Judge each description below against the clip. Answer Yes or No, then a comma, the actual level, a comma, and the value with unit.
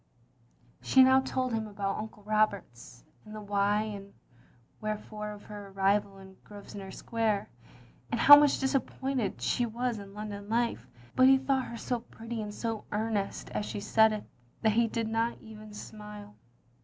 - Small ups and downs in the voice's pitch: Yes, narrow, 2.2 semitones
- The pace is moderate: Yes, average, 170 wpm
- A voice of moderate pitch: No, high, 215 Hz